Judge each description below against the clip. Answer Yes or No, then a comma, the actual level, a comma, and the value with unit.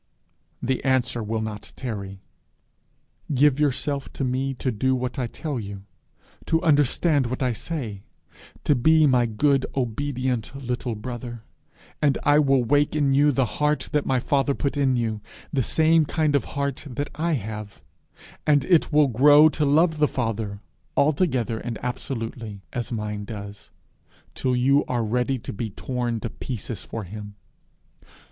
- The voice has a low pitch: Yes, low, 130 Hz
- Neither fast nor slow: Yes, average, 155 wpm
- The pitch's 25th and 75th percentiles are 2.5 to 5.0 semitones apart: Yes, average, 4.1 semitones